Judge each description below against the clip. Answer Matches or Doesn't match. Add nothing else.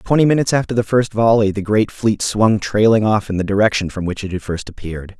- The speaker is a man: Matches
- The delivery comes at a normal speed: Doesn't match